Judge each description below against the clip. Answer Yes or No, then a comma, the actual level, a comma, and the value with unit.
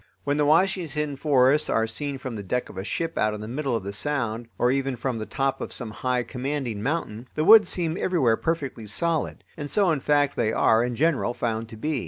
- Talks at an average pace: No, fast, 230 wpm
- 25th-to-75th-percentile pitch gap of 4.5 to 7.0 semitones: Yes, average, 4.8 semitones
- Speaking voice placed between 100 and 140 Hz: Yes, low, 135 Hz